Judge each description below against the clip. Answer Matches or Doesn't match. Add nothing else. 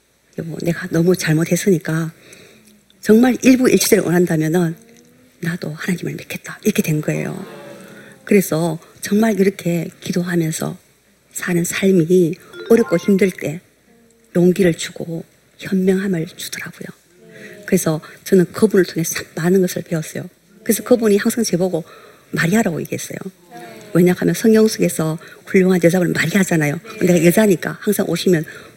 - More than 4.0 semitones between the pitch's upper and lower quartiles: Doesn't match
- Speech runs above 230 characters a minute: Matches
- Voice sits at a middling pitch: Matches